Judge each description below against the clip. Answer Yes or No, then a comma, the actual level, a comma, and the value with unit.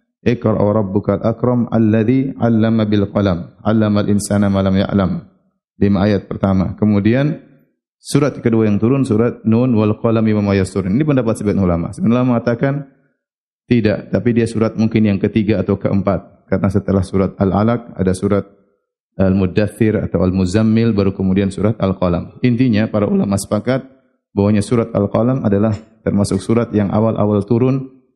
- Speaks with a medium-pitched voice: No, low, 105 Hz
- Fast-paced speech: Yes, fast, 160 wpm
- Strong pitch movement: No, average, 2.8 semitones